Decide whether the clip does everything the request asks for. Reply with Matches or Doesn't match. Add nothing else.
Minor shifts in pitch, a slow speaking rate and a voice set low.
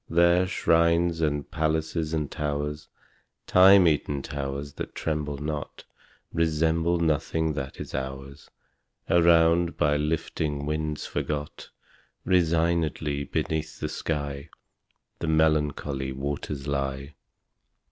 Matches